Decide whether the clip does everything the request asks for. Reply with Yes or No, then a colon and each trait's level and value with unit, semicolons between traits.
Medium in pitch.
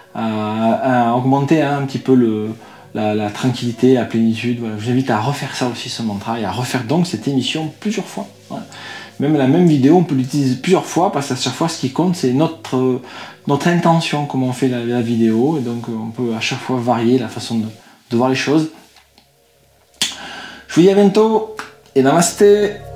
No: low, 130 Hz